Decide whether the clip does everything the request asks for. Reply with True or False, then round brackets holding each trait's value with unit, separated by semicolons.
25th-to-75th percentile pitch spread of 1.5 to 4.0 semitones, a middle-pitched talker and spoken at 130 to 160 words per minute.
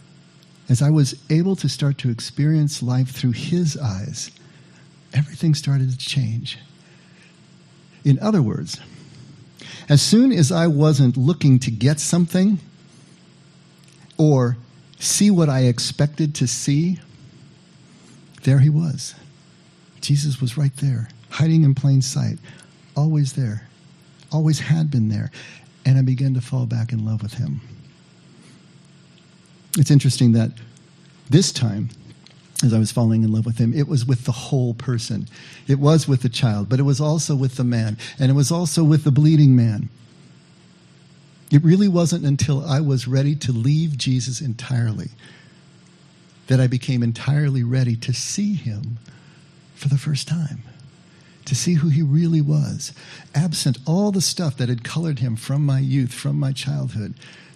True (3.7 semitones; 145 Hz; 150 wpm)